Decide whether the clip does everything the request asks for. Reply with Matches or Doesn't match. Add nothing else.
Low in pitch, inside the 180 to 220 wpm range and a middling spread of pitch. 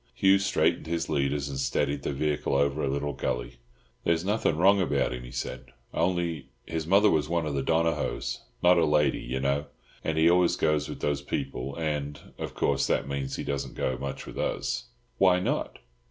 Matches